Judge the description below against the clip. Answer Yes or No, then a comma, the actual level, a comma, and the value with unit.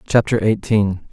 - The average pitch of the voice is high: No, low, 105 Hz